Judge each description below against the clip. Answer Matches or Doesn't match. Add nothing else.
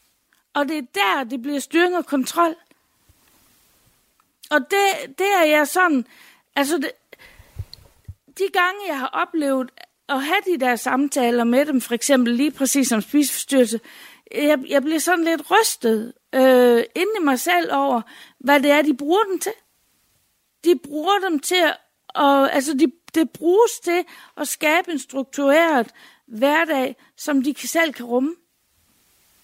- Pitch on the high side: Matches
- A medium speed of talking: Matches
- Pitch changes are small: Doesn't match